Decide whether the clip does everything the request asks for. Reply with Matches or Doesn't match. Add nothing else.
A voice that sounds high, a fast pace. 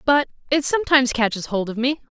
Doesn't match